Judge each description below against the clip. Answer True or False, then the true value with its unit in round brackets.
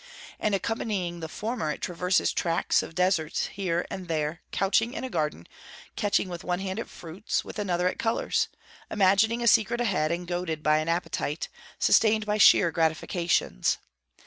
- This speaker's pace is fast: False (165 wpm)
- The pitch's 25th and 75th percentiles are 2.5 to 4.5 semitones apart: True (4.0 semitones)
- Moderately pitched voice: True (180 Hz)